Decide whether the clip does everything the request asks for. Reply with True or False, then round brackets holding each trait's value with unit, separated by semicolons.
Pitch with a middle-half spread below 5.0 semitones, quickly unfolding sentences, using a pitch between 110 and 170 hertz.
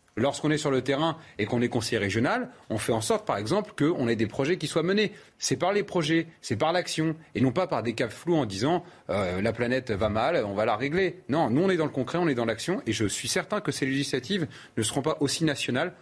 False (5.5 semitones; 265 wpm; 140 Hz)